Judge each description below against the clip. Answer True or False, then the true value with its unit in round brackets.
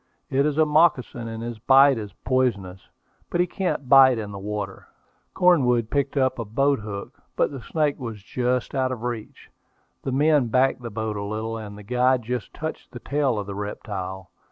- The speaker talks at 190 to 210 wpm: True (200 wpm)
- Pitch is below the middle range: True (125 Hz)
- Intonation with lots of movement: False (4.3 semitones)